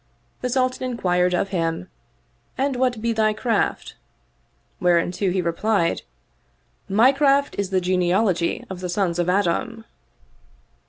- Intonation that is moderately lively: Yes, average, 4.7 semitones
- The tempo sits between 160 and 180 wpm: No, average, 150 wpm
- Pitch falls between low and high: No, high, 195 Hz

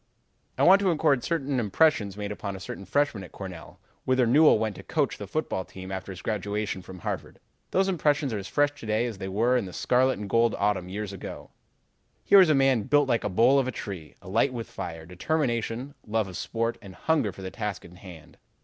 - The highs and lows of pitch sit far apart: Yes, wide, 5.8 semitones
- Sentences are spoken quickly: Yes, fast, 220 wpm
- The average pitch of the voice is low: Yes, low, 110 Hz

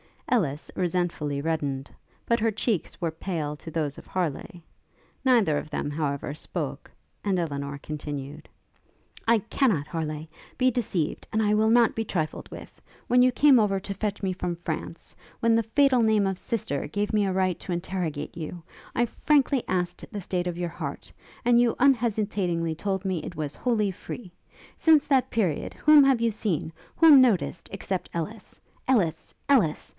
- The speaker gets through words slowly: No, average, 170 wpm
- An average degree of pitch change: No, wide, 6.1 semitones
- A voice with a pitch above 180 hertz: Yes, high, 190 Hz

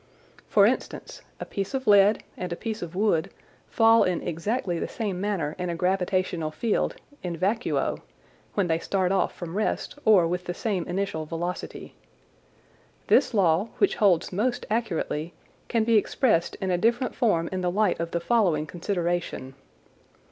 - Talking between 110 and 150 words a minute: No, average, 160 wpm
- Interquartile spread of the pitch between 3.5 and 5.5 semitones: Yes, average, 3.9 semitones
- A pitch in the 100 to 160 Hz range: No, medium, 185 Hz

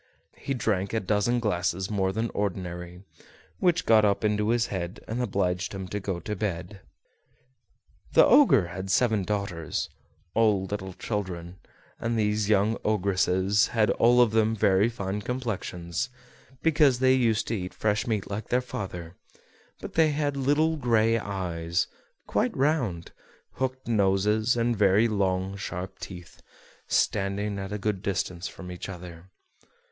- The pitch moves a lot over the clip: No, average, 3.4 semitones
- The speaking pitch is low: Yes, low, 105 Hz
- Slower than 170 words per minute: Yes, average, 145 wpm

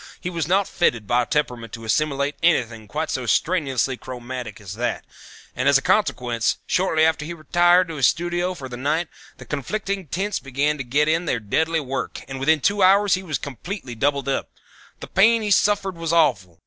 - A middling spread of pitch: No, wide, 5.7 semitones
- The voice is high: No, medium, 150 Hz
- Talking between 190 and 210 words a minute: Yes, average, 200 wpm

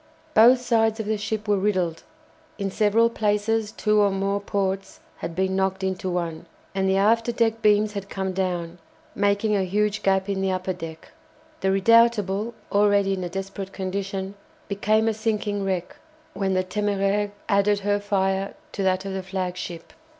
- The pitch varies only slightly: Yes, narrow, 1.7 semitones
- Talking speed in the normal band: Yes, average, 170 wpm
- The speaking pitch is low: No, high, 195 Hz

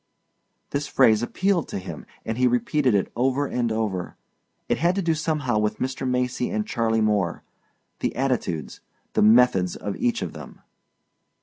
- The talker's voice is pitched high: No, low, 125 Hz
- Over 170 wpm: No, average, 165 wpm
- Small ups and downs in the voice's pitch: No, average, 4.9 semitones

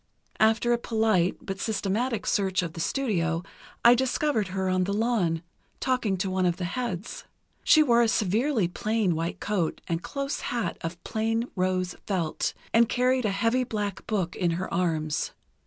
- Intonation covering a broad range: No, average, 4.6 semitones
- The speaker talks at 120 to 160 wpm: No, average, 170 wpm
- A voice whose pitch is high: Yes, high, 205 Hz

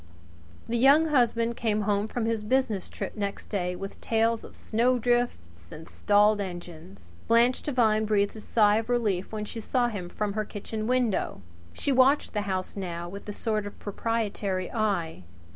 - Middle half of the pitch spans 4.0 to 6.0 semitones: No, average, 3.0 semitones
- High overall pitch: Yes, high, 215 Hz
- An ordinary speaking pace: Yes, average, 170 wpm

